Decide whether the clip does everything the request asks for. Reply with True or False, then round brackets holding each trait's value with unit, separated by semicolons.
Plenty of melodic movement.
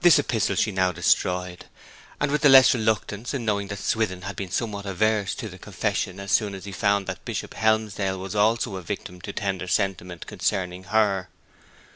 False (2.7 semitones)